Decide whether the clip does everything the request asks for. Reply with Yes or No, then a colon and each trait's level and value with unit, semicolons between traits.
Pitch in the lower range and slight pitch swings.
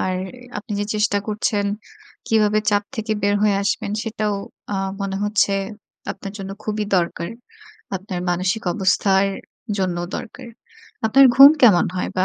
No: high, 205 Hz; narrow, 2.0 semitones